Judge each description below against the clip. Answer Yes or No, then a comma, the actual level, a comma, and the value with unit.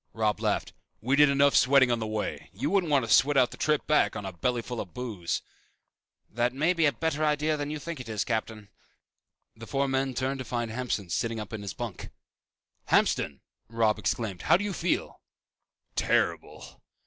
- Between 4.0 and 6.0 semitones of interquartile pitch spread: Yes, average, 4.8 semitones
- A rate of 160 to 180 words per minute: No, average, 195 wpm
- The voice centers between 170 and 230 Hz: No, low, 125 Hz